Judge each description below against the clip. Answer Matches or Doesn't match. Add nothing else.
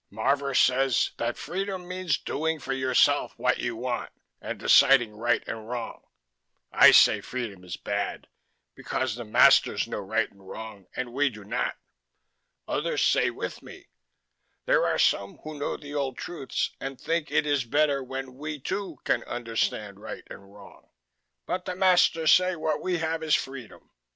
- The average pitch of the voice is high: Doesn't match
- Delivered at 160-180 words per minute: Matches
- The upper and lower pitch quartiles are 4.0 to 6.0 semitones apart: Matches